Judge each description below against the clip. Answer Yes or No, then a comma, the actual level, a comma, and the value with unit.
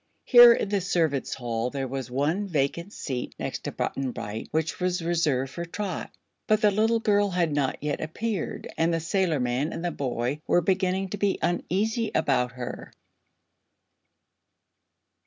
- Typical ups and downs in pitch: No, wide, 6.3 semitones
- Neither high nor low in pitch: Yes, medium, 165 Hz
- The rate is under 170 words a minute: Yes, average, 155 wpm